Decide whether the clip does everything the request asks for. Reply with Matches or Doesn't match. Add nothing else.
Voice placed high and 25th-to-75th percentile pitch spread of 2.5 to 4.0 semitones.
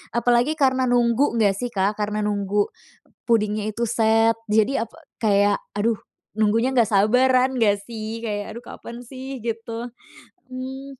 Matches